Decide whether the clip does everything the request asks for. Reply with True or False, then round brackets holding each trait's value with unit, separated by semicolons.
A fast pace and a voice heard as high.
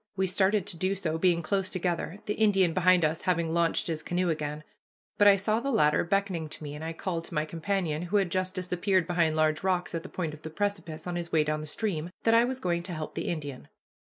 False (245 wpm; 175 Hz)